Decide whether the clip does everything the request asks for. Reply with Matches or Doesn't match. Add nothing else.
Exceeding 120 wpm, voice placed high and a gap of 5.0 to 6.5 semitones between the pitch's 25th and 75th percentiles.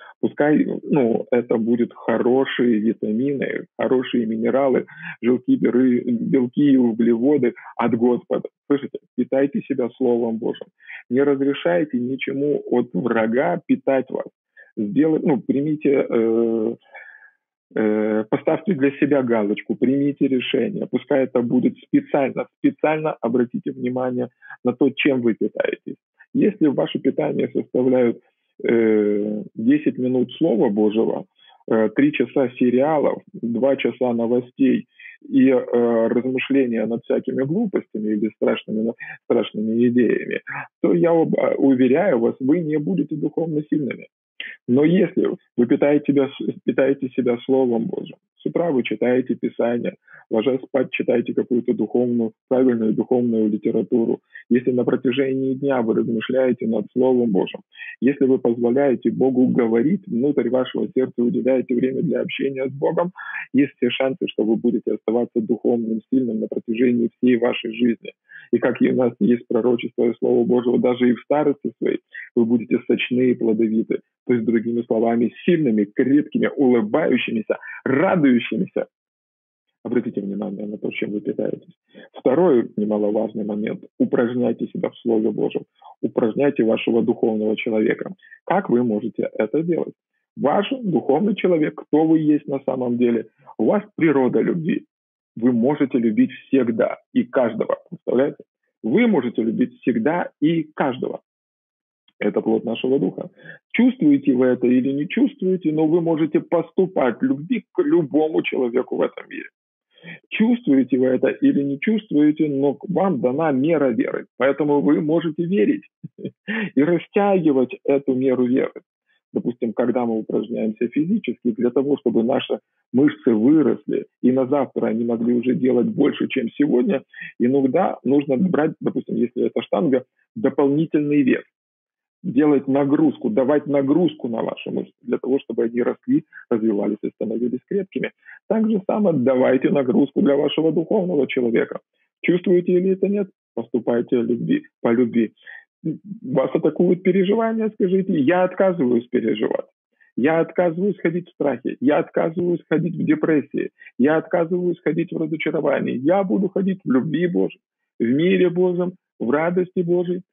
Doesn't match